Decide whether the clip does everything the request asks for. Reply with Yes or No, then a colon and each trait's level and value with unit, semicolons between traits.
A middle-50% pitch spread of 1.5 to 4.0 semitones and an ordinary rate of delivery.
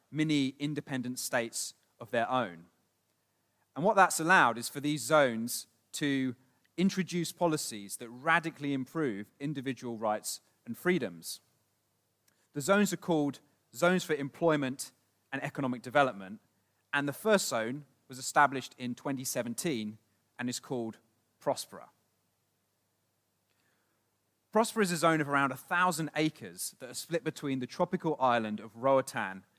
No: average, 5.3 semitones; average, 130 wpm